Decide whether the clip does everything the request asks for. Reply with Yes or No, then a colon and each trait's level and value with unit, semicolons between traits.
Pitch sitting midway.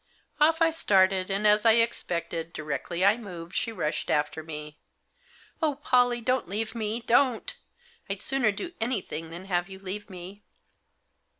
No: high, 205 Hz